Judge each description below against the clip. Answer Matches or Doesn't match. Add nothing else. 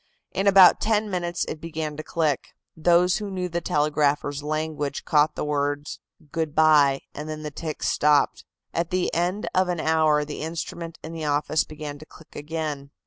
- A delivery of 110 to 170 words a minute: Doesn't match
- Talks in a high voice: Doesn't match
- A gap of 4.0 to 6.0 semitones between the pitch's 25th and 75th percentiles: Doesn't match